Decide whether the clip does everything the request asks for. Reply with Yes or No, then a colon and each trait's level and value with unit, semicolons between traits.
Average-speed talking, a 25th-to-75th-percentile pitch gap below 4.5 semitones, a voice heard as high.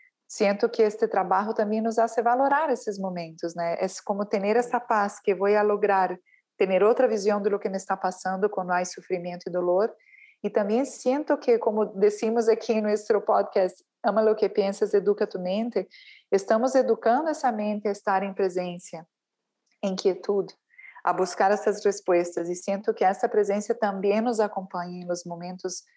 Yes: average, 170 wpm; average, 3.1 semitones; high, 205 Hz